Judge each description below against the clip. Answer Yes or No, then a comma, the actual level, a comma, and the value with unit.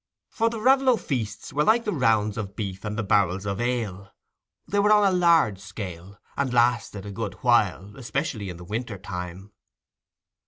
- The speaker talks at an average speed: Yes, average, 170 wpm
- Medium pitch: No, low, 110 Hz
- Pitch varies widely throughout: Yes, wide, 6.0 semitones